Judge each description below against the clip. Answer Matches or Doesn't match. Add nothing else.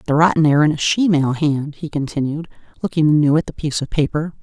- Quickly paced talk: Matches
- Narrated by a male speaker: Doesn't match